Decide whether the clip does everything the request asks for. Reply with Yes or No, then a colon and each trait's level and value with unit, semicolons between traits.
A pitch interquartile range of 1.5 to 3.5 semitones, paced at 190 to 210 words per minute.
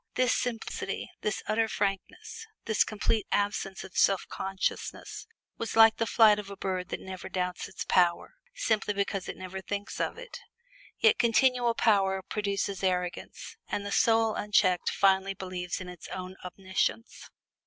No: average, 3.0 semitones; average, 155 wpm